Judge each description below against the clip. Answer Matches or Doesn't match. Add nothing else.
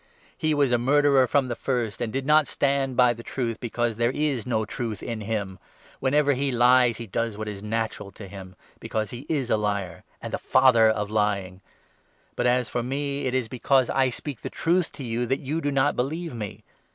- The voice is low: Matches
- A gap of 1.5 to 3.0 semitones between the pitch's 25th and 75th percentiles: Doesn't match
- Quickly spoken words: Matches